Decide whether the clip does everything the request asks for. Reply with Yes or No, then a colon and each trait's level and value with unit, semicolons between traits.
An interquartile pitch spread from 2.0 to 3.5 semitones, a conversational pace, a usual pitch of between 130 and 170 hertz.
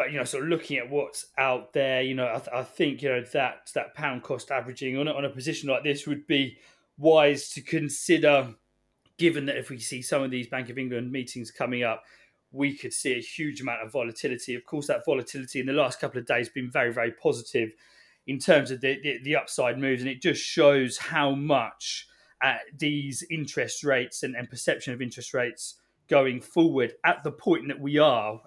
No: narrow, 2.6 semitones; fast, 215 wpm; low, 135 Hz